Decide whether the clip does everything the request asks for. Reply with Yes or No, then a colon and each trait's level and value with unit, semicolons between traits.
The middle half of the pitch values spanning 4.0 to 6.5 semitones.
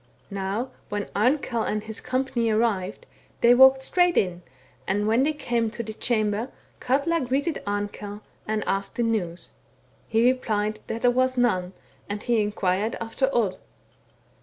No: average, 3.5 semitones